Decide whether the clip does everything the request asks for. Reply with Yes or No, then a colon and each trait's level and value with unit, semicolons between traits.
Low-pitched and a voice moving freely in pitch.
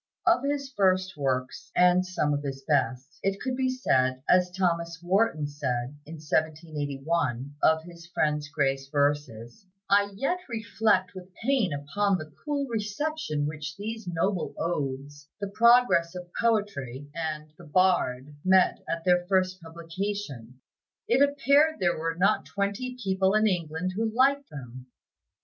No: medium, 175 Hz; wide, 5.8 semitones